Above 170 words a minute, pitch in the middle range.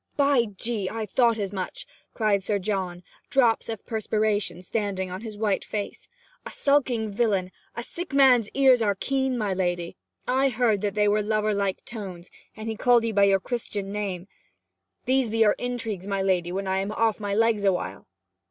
No: average, 185 wpm; high, 210 Hz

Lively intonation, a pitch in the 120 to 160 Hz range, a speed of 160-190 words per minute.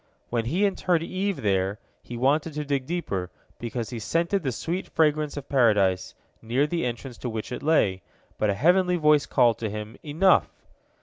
Yes: wide, 6.3 semitones; low, 135 Hz; average, 180 wpm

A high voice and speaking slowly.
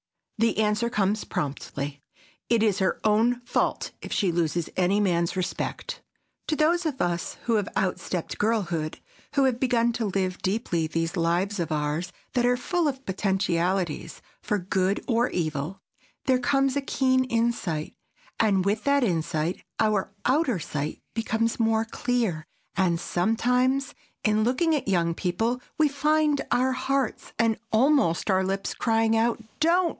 No: high, 215 Hz; average, 150 wpm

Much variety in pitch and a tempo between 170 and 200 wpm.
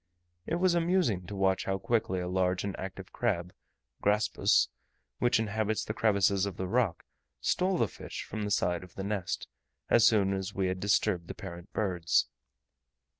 No: average, 2.9 semitones; average, 175 wpm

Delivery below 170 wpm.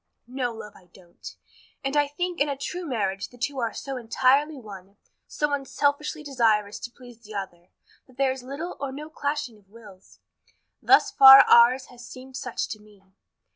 No: average, 185 wpm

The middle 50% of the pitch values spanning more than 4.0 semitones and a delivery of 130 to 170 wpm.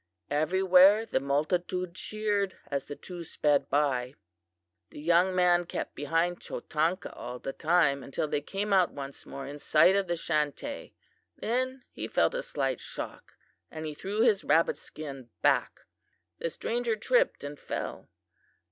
Yes: average, 5.0 semitones; average, 145 wpm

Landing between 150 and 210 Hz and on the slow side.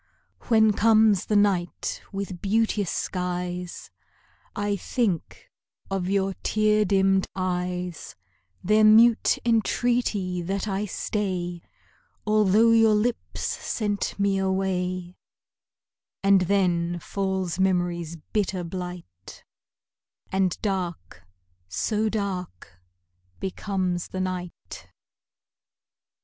Yes: high, 190 Hz; slow, 90 wpm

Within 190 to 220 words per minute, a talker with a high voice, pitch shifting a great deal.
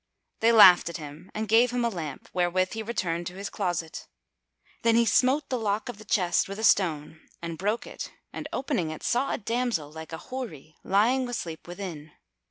Yes: average, 195 wpm; high, 195 Hz; wide, 5.7 semitones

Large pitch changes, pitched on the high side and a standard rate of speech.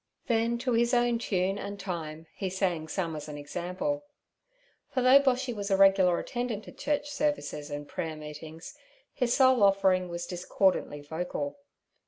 Yes: wide, 6.6 semitones; high, 195 Hz; average, 160 wpm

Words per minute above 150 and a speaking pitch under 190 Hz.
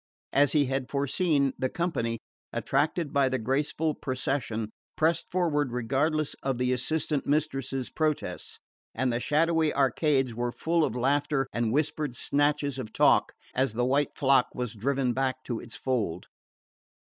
No: average, 145 wpm; low, 135 Hz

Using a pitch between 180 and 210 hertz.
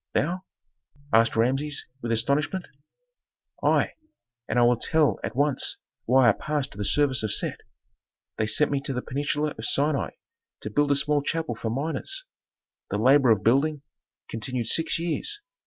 No: medium, 140 Hz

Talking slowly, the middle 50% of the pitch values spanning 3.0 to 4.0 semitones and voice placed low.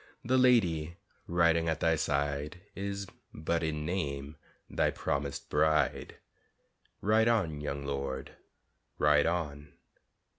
Yes: slow, 110 wpm; average, 3.4 semitones; very low, 80 Hz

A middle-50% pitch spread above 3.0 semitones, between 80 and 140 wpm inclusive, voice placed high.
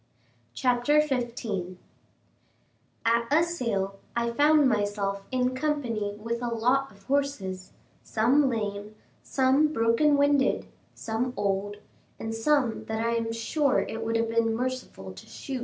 Yes: average, 4.0 semitones; slow, 135 wpm; high, 235 Hz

